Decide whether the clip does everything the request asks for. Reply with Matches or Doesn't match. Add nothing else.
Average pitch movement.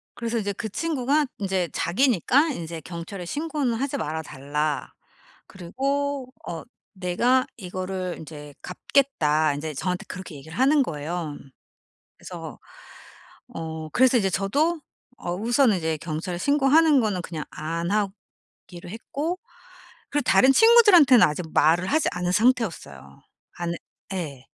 Doesn't match